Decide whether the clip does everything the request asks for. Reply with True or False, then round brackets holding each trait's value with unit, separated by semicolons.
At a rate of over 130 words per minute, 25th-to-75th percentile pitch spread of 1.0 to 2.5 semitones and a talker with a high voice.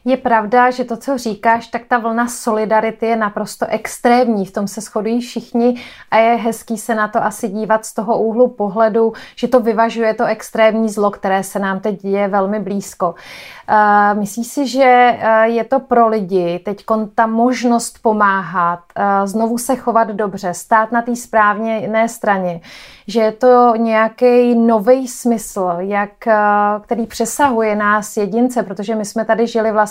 True (165 wpm; 2.0 semitones; 225 Hz)